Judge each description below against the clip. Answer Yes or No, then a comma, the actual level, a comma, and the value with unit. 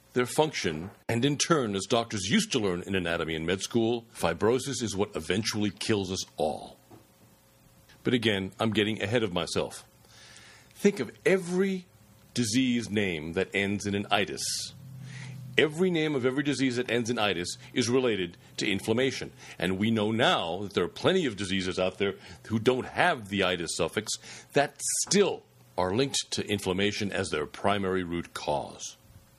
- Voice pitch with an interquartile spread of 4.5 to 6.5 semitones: Yes, average, 4.8 semitones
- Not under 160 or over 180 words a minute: Yes, average, 165 wpm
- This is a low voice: Yes, low, 110 Hz